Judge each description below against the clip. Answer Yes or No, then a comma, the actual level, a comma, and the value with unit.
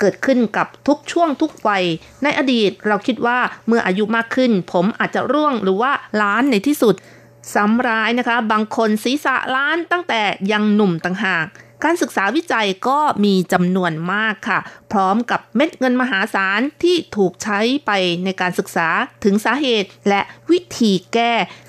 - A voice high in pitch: Yes, high, 220 Hz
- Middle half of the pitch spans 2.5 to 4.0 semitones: No, average, 5.0 semitones